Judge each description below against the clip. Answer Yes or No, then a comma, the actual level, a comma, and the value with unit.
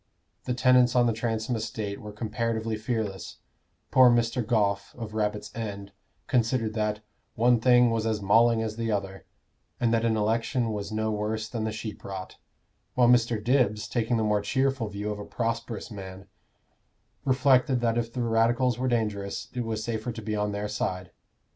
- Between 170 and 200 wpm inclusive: Yes, average, 175 wpm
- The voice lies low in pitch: Yes, low, 110 Hz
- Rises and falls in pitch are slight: Yes, narrow, 2.1 semitones